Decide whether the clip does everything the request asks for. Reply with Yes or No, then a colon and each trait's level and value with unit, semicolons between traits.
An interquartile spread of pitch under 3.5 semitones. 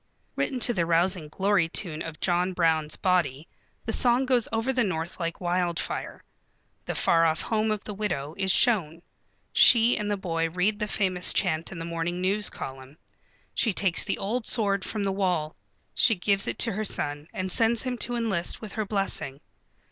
No: average, 4.4 semitones